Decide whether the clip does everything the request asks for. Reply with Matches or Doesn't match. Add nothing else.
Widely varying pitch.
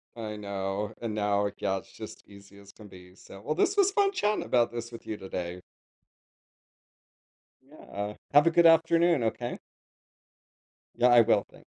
Matches